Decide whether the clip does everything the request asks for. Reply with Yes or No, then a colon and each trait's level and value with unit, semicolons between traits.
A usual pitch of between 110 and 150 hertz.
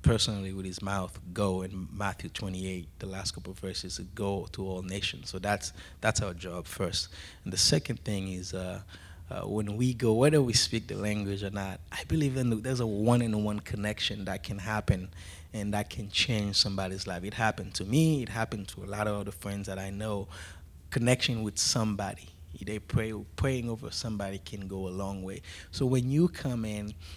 No: low, 100 Hz